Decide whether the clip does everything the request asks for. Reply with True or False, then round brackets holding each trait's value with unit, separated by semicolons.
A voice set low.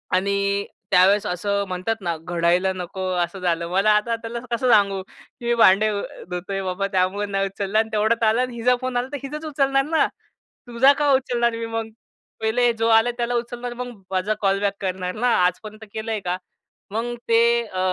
False (215 Hz)